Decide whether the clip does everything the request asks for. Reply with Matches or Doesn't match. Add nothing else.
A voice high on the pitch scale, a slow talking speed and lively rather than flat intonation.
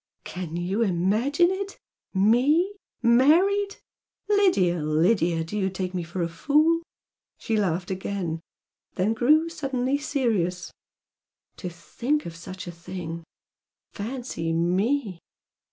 Matches